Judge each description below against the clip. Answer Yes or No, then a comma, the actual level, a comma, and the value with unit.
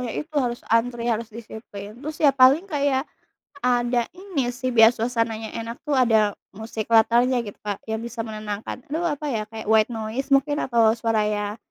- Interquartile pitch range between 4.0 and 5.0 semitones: No, average, 2.9 semitones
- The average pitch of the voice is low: No, high, 235 Hz